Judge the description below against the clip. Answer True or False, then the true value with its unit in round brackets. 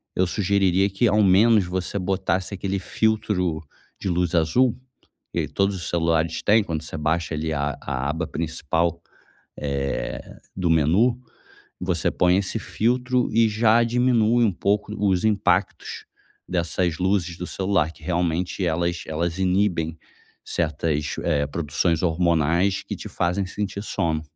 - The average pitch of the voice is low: True (90 Hz)